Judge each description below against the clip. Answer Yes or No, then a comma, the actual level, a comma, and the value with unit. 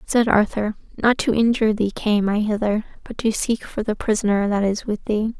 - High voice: Yes, high, 215 Hz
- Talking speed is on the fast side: Yes, fast, 210 wpm